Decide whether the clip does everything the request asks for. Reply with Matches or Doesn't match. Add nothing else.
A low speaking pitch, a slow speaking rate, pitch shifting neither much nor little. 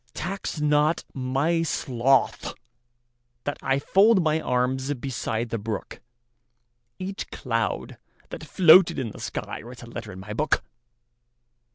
Matches